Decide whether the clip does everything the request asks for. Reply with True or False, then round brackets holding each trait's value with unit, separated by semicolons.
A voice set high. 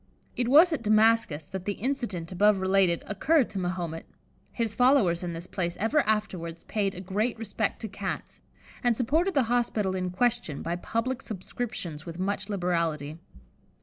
True (200 Hz)